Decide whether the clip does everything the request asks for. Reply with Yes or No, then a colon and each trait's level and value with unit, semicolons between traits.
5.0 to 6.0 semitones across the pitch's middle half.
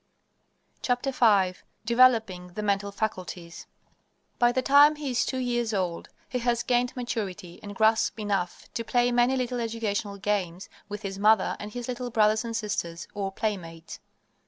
No: average, 3.7 semitones